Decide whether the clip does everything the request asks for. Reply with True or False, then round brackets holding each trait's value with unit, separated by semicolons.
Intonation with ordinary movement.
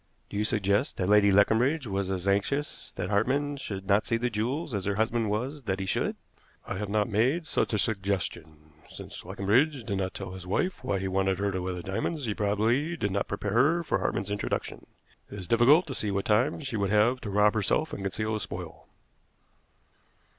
True (4.0 semitones)